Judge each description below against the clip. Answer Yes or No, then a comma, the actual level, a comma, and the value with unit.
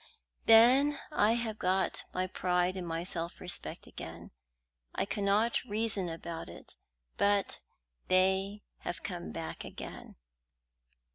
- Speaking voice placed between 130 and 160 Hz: No, high, 190 Hz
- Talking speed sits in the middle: No, slow, 125 wpm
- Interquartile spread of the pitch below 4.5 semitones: Yes, average, 3.3 semitones